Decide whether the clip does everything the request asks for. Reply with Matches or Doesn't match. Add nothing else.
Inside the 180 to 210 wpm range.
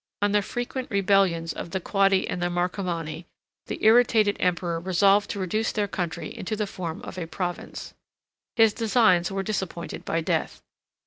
Doesn't match